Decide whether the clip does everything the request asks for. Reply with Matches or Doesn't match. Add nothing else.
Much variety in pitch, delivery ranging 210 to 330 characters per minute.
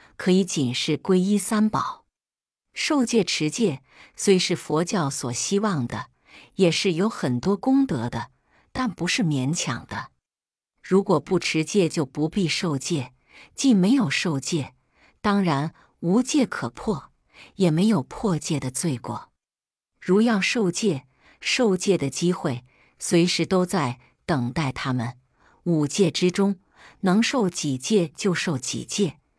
Doesn't match